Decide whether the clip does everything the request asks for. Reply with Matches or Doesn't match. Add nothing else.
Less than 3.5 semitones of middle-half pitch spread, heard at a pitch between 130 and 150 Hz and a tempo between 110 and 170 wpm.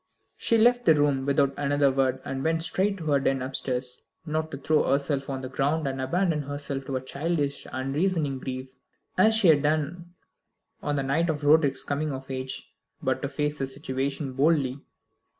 Doesn't match